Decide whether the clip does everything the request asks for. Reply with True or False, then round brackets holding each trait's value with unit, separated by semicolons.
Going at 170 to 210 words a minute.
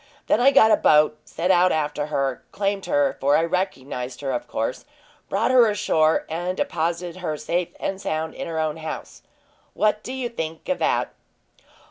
True (180 wpm)